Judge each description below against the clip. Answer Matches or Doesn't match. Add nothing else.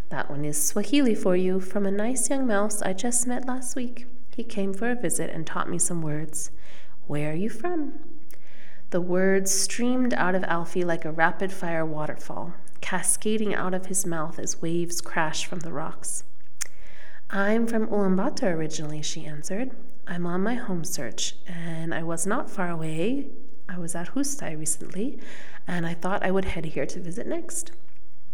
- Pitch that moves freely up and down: Matches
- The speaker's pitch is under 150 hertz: Doesn't match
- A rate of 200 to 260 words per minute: Doesn't match